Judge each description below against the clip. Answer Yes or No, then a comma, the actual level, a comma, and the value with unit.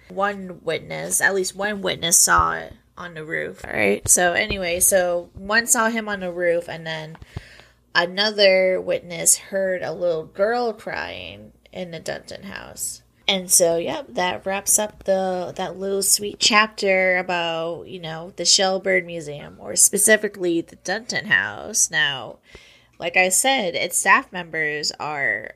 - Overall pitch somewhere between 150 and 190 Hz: Yes, medium, 185 Hz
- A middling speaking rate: Yes, average, 155 wpm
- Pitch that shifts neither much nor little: Yes, average, 3.2 semitones